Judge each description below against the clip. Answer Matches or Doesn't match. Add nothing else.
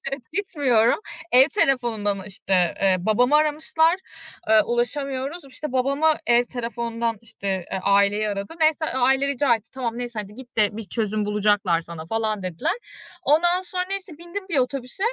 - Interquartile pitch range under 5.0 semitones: Doesn't match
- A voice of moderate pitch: Doesn't match